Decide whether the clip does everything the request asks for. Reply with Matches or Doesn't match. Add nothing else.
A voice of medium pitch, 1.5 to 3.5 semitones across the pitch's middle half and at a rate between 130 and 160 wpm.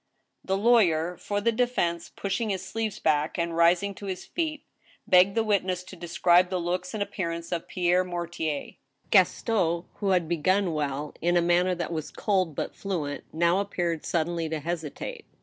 Doesn't match